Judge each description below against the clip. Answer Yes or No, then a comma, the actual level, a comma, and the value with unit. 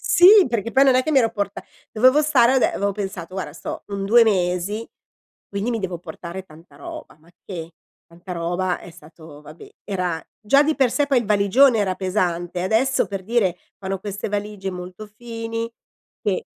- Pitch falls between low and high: No, high, 200 Hz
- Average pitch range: Yes, average, 4.7 semitones